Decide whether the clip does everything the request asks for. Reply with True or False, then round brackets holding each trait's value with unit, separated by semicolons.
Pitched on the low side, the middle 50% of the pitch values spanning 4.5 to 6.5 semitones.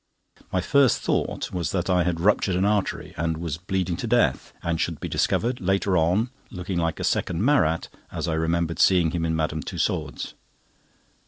False (90 Hz; 2.9 semitones)